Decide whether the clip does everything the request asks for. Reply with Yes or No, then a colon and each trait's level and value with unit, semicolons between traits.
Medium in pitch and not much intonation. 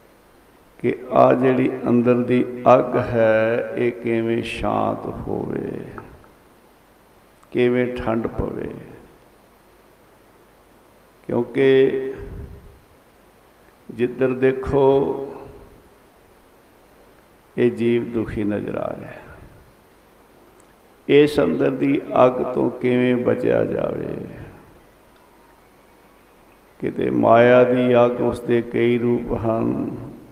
No: low, 120 Hz; narrow, 1.3 semitones